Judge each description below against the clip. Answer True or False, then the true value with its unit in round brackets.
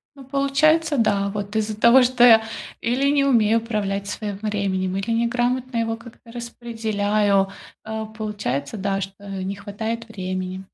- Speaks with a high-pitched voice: True (220 Hz)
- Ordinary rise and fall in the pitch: True (3.0 semitones)